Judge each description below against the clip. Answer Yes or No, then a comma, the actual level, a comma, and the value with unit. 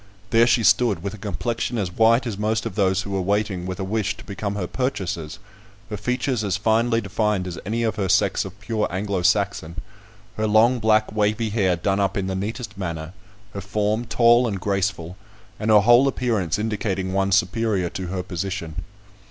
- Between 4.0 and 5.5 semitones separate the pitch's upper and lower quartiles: No, average, 2.8 semitones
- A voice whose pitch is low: Yes, low, 105 Hz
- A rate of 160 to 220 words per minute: Yes, average, 195 wpm